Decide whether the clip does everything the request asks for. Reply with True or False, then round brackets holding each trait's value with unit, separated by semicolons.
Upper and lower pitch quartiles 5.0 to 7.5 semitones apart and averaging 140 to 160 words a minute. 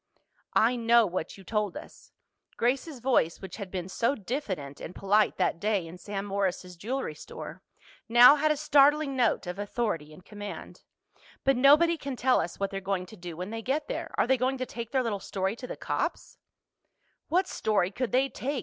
False (5.5 semitones; 195 wpm)